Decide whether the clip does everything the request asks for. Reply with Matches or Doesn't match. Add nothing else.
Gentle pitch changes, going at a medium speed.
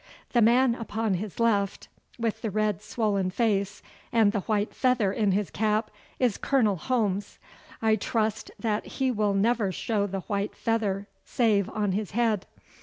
Matches